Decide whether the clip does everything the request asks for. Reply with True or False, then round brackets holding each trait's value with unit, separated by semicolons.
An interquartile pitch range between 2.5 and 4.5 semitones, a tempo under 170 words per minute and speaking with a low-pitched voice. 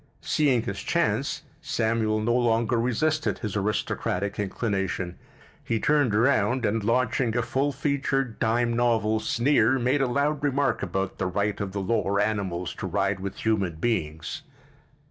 True (3.9 semitones; 145 wpm; 115 Hz)